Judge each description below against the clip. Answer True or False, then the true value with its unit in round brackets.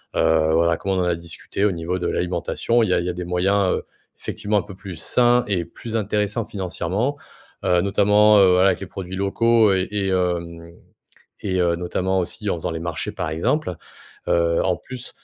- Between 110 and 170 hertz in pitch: False (95 Hz)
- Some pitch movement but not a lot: True (3.0 semitones)